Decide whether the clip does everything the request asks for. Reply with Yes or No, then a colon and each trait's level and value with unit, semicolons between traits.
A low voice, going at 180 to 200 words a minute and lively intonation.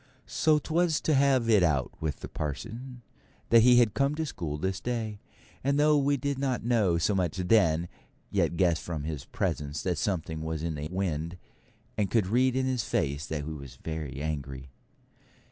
Yes: very low, 95 Hz; average, 185 wpm; wide, 8.2 semitones